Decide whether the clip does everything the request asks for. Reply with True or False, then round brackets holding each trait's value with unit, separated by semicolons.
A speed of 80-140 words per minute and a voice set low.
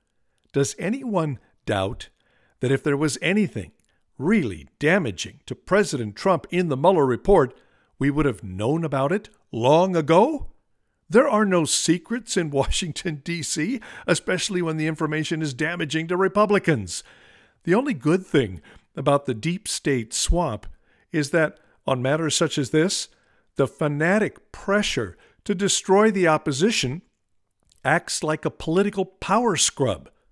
False (135 wpm; 160 Hz)